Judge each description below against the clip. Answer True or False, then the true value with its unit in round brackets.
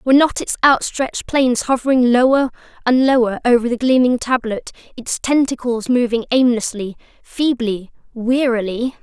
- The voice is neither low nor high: False (245 Hz)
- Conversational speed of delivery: False (120 wpm)